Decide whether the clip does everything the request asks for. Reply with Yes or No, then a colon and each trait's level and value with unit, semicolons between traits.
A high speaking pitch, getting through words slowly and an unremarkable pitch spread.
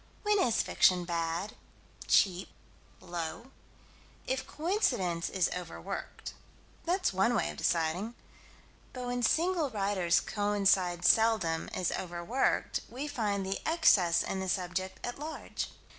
No: high, 195 Hz; slow, 120 wpm; wide, 5.8 semitones